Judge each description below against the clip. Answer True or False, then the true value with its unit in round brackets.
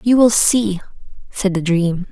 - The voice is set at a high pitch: True (200 Hz)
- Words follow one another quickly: False (170 wpm)